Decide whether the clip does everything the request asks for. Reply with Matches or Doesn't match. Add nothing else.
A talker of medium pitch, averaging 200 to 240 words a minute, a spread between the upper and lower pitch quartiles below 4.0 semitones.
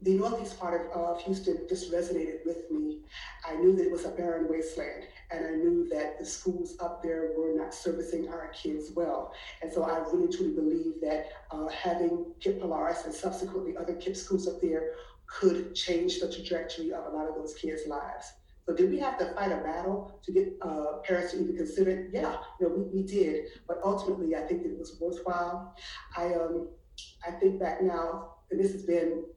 Matches